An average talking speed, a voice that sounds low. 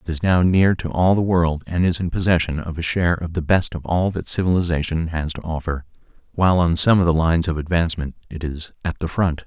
No: fast, 240 wpm; very low, 85 Hz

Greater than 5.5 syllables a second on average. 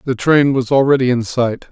No: 5.2 syllables/s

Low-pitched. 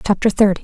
No: high, 200 Hz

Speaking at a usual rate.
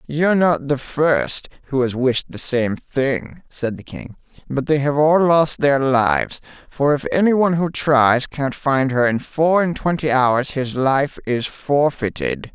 Yes: average, 180 wpm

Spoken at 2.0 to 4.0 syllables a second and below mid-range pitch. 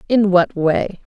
No: 3.5 syllables/s; high, 190 Hz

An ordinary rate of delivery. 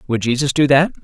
No: fast, 235 wpm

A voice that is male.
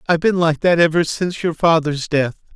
Yes: male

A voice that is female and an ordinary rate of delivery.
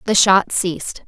Yes: female; average, 165 wpm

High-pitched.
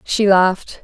Yes: high, 195 Hz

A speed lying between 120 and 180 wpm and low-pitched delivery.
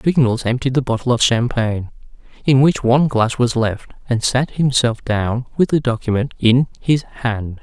Yes: average, 175 wpm; low, 125 Hz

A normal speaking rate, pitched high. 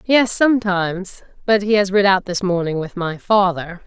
Yes: average, 185 wpm; high, 195 Hz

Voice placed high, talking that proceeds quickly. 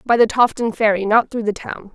Yes: high, 220 Hz; fast, 245 wpm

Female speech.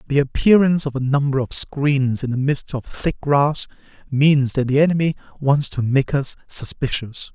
No: male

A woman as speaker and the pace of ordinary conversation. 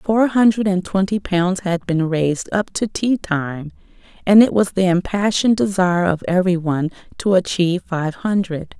Yes: female; average, 165 wpm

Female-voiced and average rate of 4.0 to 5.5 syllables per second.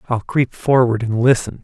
No: male; 4.9 syllables/s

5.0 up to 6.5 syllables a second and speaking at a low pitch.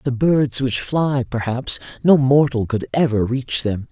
No: 4.0 syllables/s; low, 130 Hz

